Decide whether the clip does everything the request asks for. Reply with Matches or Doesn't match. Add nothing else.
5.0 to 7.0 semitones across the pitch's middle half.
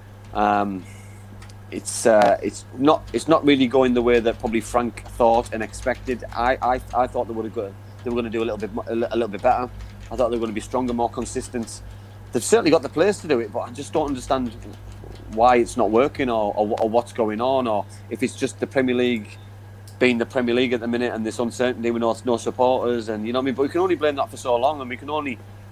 Doesn't match